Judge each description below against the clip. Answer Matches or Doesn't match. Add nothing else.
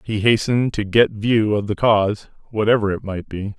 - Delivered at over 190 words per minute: Matches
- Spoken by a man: Matches